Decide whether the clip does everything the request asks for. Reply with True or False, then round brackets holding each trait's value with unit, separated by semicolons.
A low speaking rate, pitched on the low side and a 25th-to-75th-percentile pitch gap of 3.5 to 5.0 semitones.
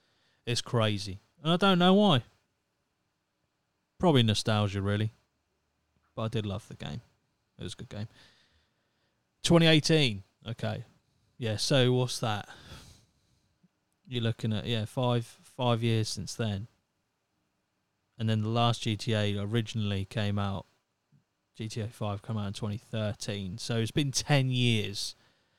False (130 wpm; 110 Hz; 2.8 semitones)